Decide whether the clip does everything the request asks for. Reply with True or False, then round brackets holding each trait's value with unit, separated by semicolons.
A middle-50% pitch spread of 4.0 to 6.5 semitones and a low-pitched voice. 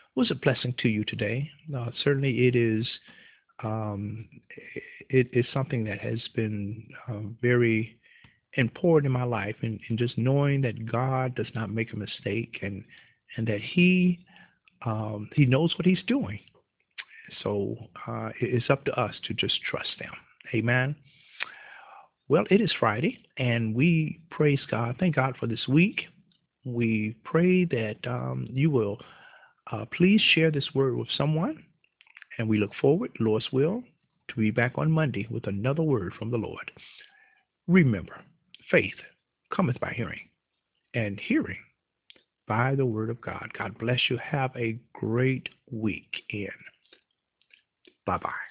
True (5.6 semitones; 125 Hz)